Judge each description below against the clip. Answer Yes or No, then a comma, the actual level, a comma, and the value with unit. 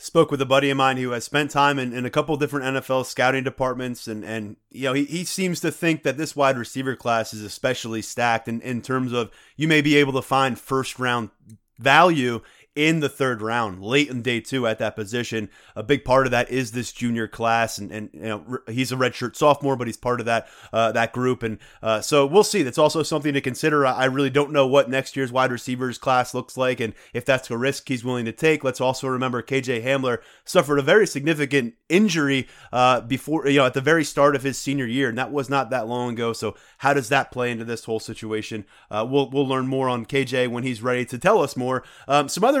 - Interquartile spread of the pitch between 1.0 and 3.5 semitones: Yes, average, 2.8 semitones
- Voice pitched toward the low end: Yes, low, 130 Hz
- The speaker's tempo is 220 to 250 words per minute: Yes, fast, 240 wpm